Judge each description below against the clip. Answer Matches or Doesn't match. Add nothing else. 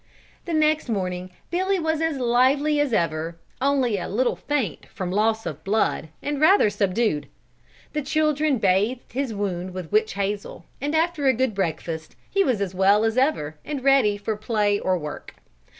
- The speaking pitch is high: Matches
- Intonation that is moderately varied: Doesn't match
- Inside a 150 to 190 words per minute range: Matches